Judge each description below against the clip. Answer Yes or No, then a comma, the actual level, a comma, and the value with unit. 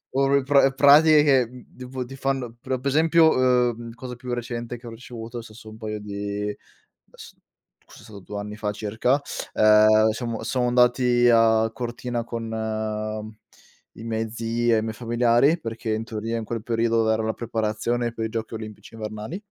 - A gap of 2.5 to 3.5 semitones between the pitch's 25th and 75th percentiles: No, narrow, 2.0 semitones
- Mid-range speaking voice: No, low, 115 Hz